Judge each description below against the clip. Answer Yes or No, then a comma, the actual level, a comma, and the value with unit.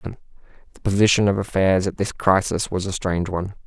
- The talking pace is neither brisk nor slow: Yes, average, 180 wpm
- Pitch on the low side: Yes, very low, 95 Hz